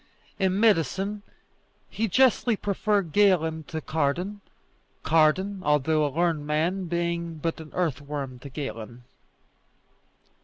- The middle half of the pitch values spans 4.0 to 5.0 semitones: Yes, average, 4.4 semitones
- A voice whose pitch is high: No, medium, 165 Hz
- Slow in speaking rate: Yes, slow, 110 wpm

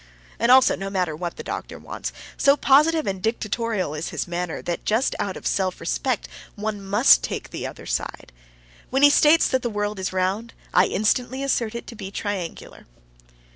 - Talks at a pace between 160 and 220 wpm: Yes, average, 185 wpm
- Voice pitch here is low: No, high, 210 Hz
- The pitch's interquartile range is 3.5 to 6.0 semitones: Yes, average, 5.0 semitones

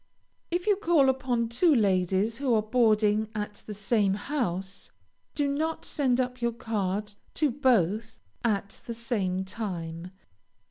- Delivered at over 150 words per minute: No, average, 140 wpm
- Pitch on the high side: Yes, high, 225 Hz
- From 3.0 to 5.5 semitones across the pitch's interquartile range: Yes, average, 4.5 semitones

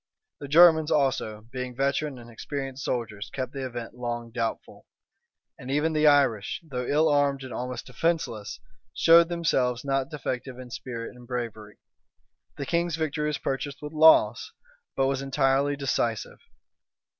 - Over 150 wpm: No, average, 145 wpm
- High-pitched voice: No, low, 135 Hz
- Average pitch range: Yes, average, 3.2 semitones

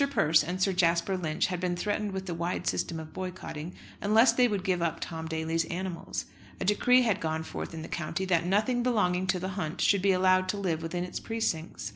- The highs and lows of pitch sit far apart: No, average, 2.8 semitones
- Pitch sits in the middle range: Yes, medium, 180 Hz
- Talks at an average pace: No, fast, 220 wpm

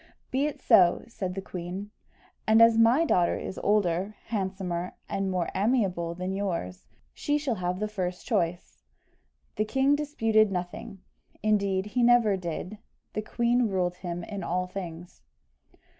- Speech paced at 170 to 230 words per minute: No, average, 145 wpm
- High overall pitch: Yes, high, 195 Hz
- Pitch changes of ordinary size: Yes, average, 3.8 semitones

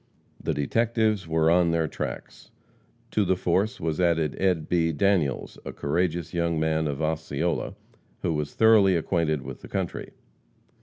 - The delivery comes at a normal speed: Yes, average, 150 wpm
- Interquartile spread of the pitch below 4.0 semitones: Yes, average, 2.8 semitones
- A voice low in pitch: Yes, very low, 85 Hz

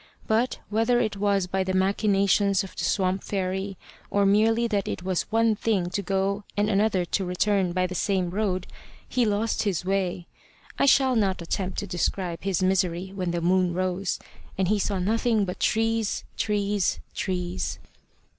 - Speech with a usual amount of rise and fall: No, narrow, 2.3 semitones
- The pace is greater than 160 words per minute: Yes, average, 170 wpm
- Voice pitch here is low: No, high, 195 Hz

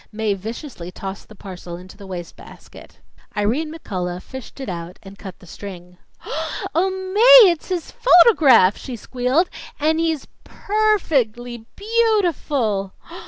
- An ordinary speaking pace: Yes, average, 145 wpm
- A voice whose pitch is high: Yes, high, 245 Hz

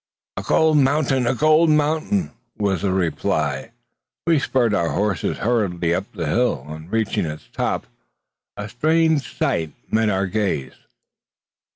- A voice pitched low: Yes, low, 105 Hz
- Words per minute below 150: Yes, average, 140 wpm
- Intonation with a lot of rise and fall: Yes, wide, 8.9 semitones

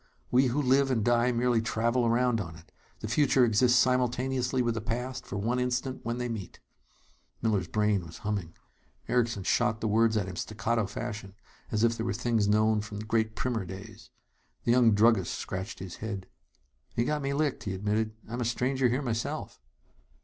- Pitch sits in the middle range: No, low, 115 Hz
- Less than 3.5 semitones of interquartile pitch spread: Yes, average, 2.9 semitones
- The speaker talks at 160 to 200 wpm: Yes, average, 185 wpm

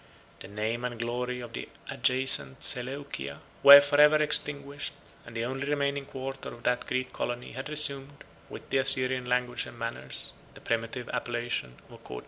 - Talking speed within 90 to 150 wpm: No, average, 160 wpm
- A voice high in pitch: No, low, 125 Hz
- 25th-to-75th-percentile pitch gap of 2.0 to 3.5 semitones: Yes, average, 2.8 semitones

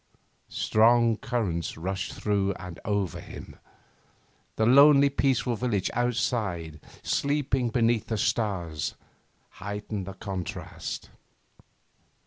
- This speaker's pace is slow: Yes, slow, 95 wpm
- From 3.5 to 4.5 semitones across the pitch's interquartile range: Yes, average, 4.1 semitones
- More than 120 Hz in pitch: No, low, 110 Hz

